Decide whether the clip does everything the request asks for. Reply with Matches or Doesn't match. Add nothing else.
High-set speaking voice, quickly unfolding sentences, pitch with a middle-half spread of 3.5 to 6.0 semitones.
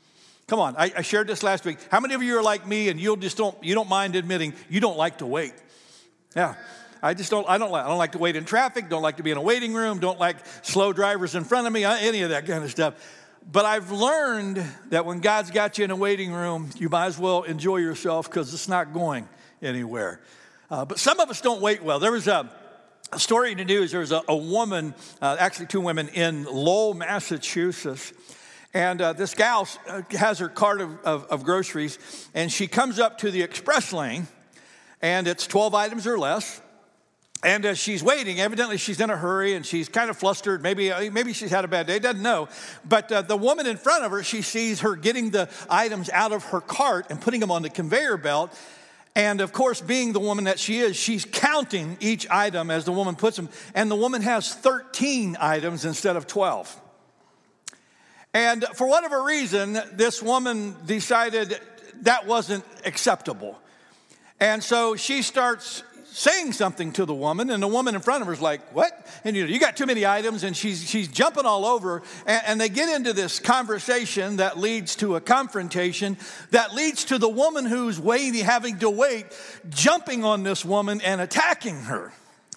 Matches